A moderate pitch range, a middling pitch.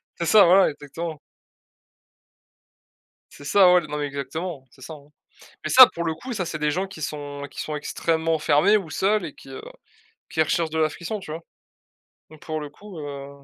Yes: average, 3.2 semitones; medium, 160 Hz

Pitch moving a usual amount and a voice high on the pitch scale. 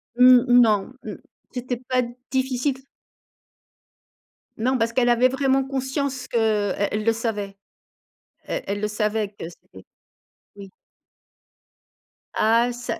Yes: average, 3.4 semitones; high, 240 Hz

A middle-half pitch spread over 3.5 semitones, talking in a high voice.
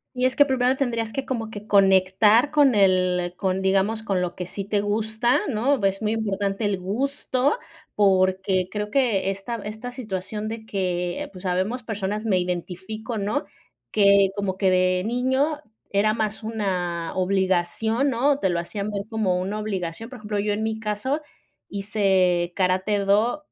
No: average, 3.0 semitones; high, 205 Hz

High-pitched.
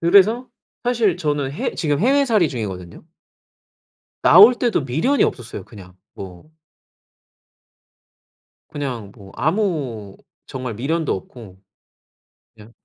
No: medium, 145 Hz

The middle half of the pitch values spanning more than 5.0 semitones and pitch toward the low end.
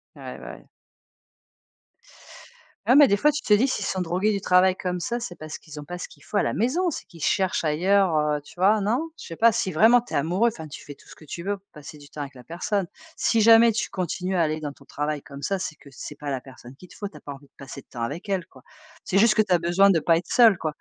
No: wide, 5.6 semitones; medium, 180 Hz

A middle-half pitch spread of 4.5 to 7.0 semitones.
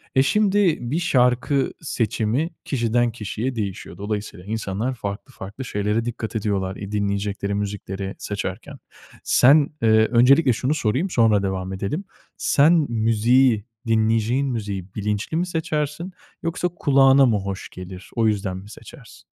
Yes: average, 4.9 semitones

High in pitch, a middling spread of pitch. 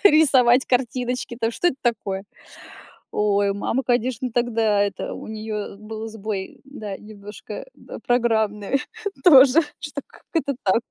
Yes: high, 225 Hz; average, 3.4 semitones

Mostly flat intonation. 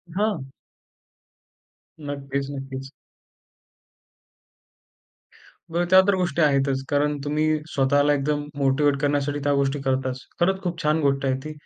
Yes: narrow, 2.0 semitones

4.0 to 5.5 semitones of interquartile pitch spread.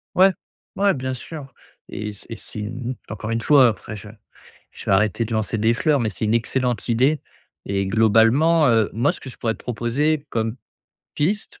Yes: average, 4.3 semitones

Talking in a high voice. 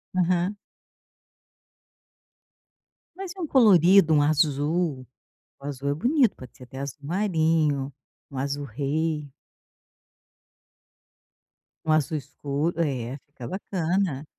No: medium, 155 Hz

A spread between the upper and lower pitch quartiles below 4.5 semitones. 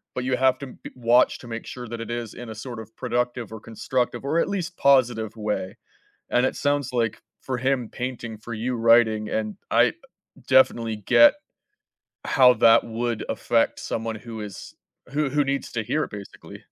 Yes: narrow, 2.5 semitones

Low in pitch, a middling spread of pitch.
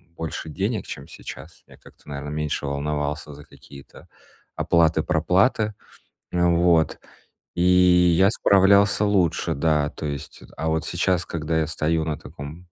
Yes: very low, 80 Hz; average, 3.2 semitones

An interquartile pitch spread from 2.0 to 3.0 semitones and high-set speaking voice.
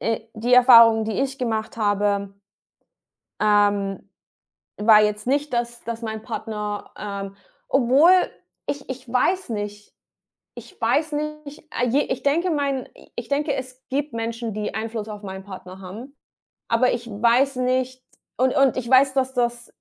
No: average, 3.8 semitones; high, 235 Hz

